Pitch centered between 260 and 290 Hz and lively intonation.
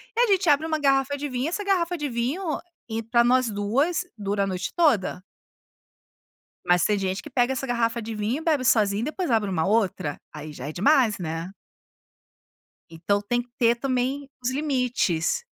No: high, 240 Hz; wide, 5.9 semitones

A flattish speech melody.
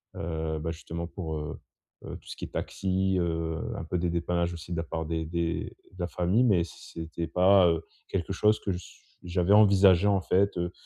Yes: narrow, 2.3 semitones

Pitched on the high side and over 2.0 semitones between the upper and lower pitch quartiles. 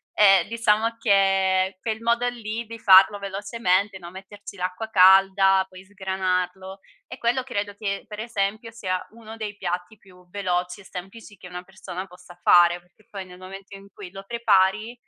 Yes: high, 195 Hz; narrow, 2.6 semitones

